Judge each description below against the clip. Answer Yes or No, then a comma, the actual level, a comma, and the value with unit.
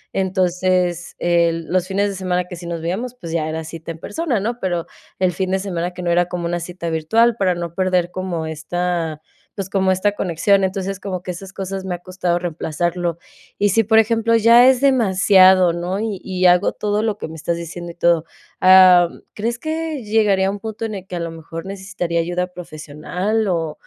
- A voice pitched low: No, medium, 185 Hz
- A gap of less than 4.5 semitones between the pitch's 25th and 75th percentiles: Yes, narrow, 2.6 semitones